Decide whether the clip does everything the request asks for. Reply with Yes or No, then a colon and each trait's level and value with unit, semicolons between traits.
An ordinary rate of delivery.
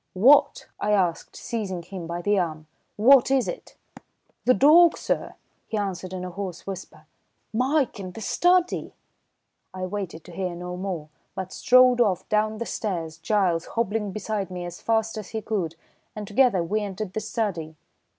Yes: average, 170 wpm